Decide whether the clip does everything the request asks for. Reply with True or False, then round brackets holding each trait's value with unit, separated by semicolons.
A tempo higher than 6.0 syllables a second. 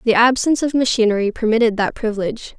True (6.9 syllables/s)